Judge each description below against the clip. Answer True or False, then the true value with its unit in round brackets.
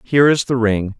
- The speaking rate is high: True (240 wpm)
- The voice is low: True (120 Hz)